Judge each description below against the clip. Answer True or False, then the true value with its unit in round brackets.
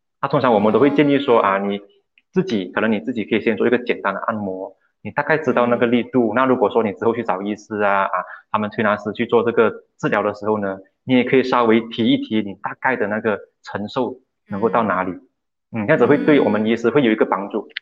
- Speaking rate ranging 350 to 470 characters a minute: True (355 characters per minute)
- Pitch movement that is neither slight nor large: True (4.0 semitones)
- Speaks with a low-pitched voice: True (115 Hz)